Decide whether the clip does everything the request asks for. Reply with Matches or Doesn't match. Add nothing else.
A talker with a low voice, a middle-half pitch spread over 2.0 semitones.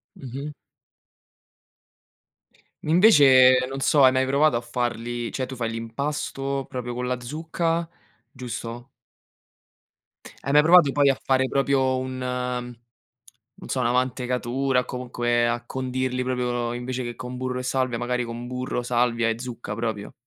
Doesn't match